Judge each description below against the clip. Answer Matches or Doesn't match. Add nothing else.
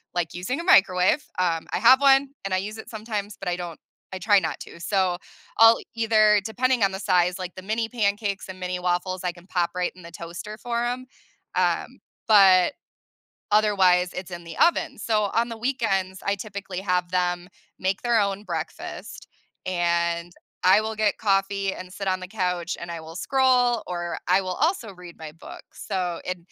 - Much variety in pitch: Doesn't match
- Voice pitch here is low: Doesn't match